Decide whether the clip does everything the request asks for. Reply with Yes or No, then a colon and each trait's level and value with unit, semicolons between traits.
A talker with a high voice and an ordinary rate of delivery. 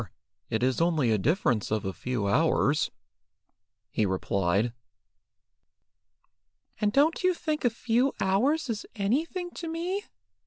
No: high, 195 Hz; slow, 125 wpm